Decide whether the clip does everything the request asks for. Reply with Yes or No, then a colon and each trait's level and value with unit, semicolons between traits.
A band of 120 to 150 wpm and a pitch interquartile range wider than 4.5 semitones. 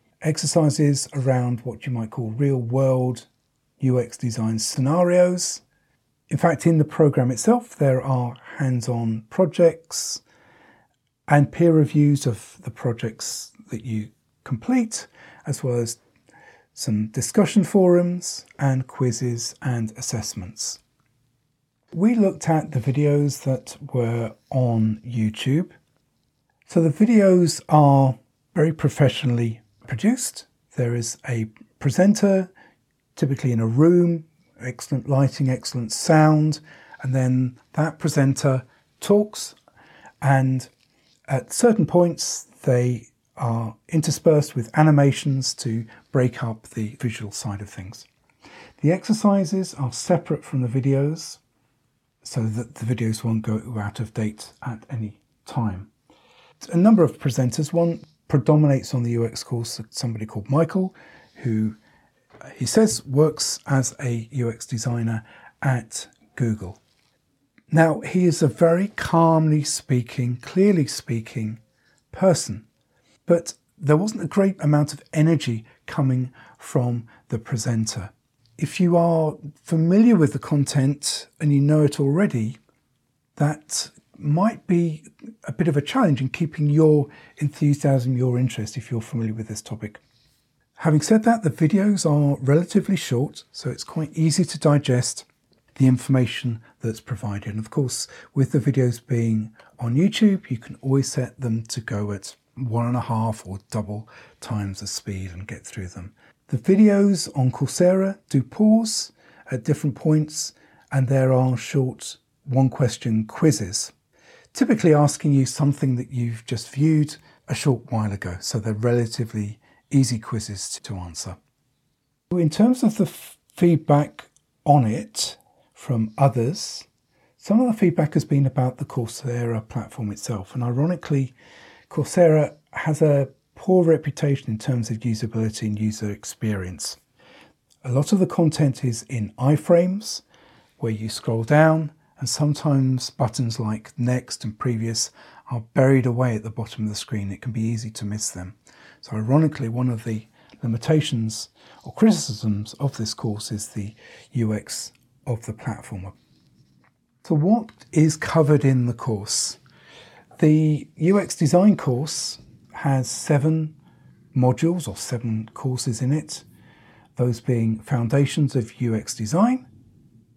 Yes: slow, 135 wpm; average, 4.9 semitones